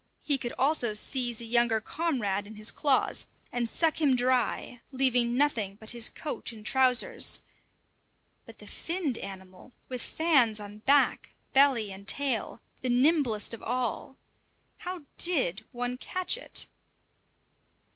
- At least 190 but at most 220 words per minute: No, slow, 135 wpm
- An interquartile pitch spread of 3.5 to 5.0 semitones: Yes, average, 4.3 semitones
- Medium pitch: No, high, 245 Hz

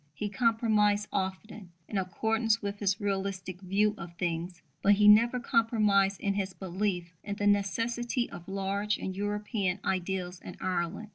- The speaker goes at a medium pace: Yes, average, 150 wpm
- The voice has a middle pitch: No, high, 200 Hz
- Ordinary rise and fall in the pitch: No, narrow, 2.1 semitones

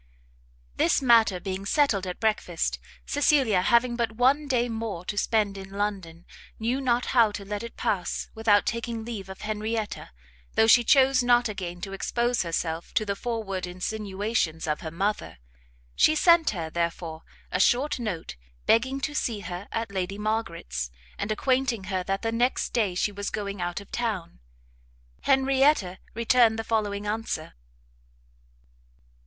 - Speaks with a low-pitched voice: No, high, 215 Hz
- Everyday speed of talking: Yes, average, 155 wpm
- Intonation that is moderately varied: Yes, average, 3.9 semitones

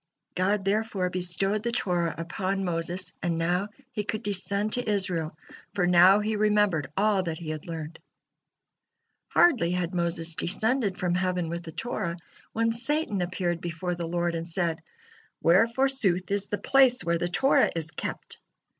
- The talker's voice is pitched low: No, medium, 185 Hz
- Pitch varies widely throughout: No, average, 3.5 semitones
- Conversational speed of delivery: Yes, average, 160 wpm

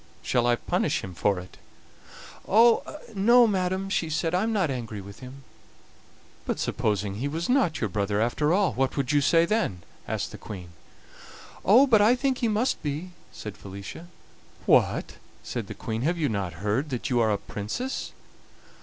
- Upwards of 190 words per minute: No, average, 180 wpm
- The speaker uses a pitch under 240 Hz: Yes, medium, 140 Hz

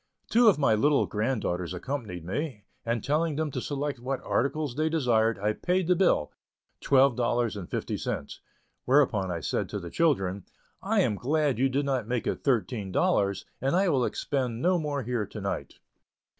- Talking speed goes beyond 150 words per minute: Yes, average, 185 wpm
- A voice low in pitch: Yes, low, 130 Hz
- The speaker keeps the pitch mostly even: No, wide, 5.5 semitones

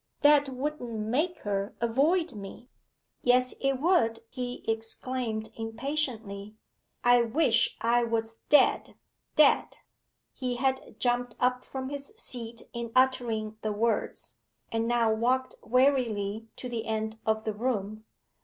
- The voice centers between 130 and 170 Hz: No, high, 235 Hz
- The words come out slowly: Yes, slow, 125 wpm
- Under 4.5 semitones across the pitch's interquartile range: Yes, average, 2.8 semitones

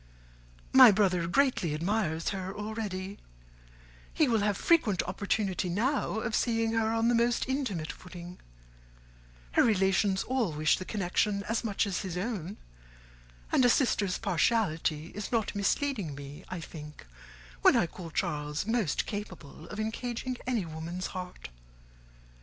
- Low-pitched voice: No, high, 200 Hz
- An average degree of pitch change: Yes, average, 4.5 semitones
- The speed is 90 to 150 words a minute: Yes, average, 140 wpm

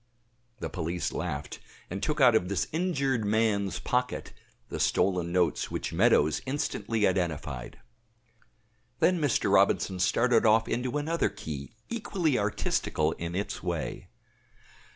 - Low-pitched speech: Yes, low, 105 Hz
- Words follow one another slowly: Yes, slow, 125 wpm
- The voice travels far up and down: Yes, wide, 6.3 semitones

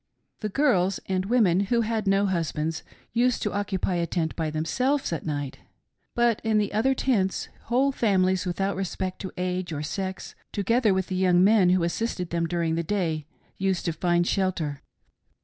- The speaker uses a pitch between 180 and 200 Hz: Yes, high, 190 Hz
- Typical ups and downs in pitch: Yes, average, 3.7 semitones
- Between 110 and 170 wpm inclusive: No, average, 185 wpm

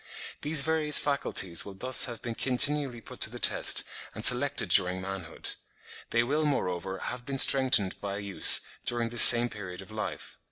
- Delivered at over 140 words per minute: Yes, average, 170 wpm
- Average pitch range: No, wide, 5.8 semitones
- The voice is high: No, low, 120 Hz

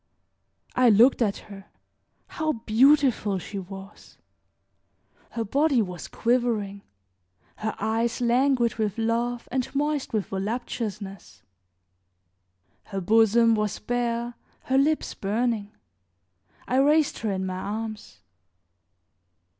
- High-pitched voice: Yes, high, 225 Hz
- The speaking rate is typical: No, slow, 105 wpm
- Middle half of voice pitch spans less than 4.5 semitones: Yes, average, 3.4 semitones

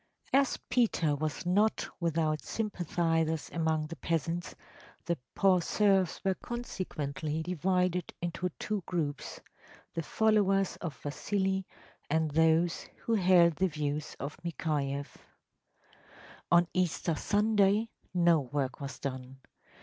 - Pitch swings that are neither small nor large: Yes, average, 3.7 semitones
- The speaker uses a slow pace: Yes, slow, 115 wpm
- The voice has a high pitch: No, medium, 170 Hz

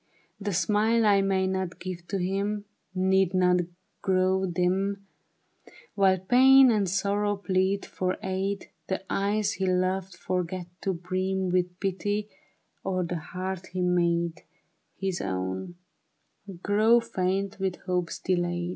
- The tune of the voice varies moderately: No, narrow, 1.8 semitones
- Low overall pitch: No, high, 190 Hz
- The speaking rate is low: Yes, slow, 130 wpm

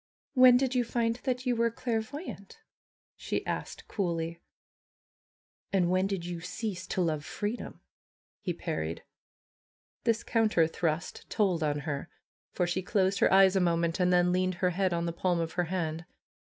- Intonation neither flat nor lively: Yes, average, 4.5 semitones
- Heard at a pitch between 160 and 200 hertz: Yes, medium, 185 Hz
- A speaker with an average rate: Yes, average, 165 wpm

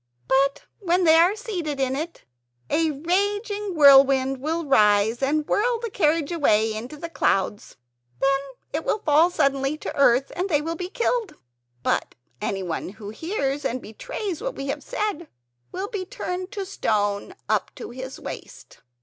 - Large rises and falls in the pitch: Yes, wide, 5.7 semitones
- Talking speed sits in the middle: Yes, average, 160 wpm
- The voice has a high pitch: Yes, very high, 305 Hz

